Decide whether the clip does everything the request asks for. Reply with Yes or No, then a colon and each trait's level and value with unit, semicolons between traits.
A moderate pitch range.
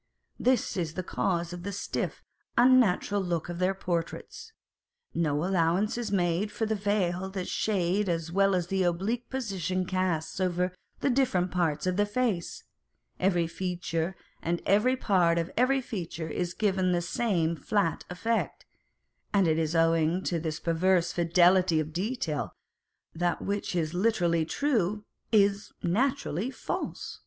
Yes: average, 3.3 semitones